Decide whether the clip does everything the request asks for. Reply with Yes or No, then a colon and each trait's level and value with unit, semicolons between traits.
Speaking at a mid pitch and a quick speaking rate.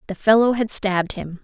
No: high, 205 Hz; fast, 210 wpm